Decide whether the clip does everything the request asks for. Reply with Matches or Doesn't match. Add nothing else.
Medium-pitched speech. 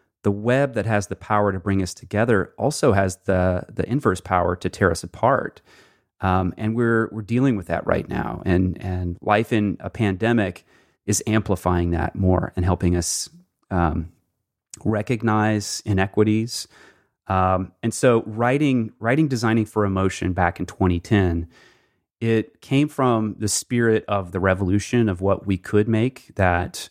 Doesn't match